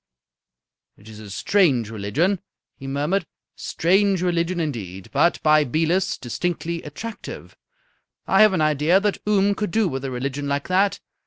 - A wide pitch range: Yes, wide, 6.0 semitones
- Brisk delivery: No, average, 155 wpm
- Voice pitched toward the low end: No, medium, 165 Hz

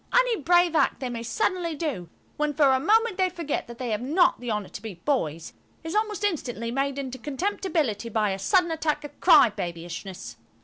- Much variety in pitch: Yes, wide, 7.6 semitones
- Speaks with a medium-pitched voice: No, very high, 280 Hz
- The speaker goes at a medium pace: Yes, average, 190 wpm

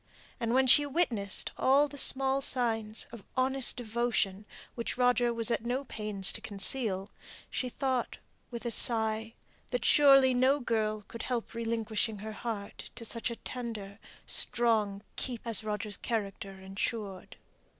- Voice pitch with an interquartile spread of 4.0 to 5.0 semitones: No, average, 2.9 semitones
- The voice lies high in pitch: Yes, high, 230 Hz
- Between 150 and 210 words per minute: No, average, 140 wpm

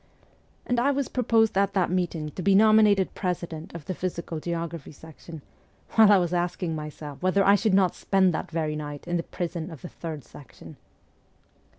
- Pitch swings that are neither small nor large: Yes, average, 3.5 semitones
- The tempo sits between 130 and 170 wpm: No, average, 185 wpm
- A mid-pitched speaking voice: Yes, medium, 175 Hz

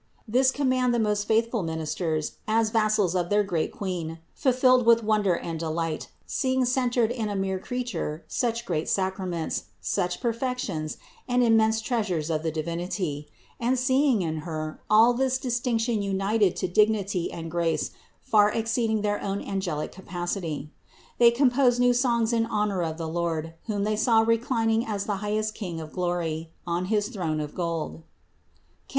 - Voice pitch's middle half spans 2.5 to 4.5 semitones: No, wide, 5.5 semitones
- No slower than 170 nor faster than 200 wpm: No, average, 160 wpm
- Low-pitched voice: No, high, 205 Hz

